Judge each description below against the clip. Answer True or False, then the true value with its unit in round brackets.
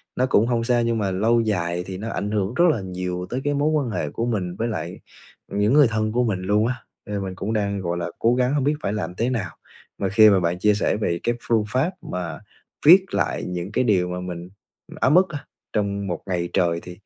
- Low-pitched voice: True (105 Hz)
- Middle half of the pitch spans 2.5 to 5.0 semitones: True (4.6 semitones)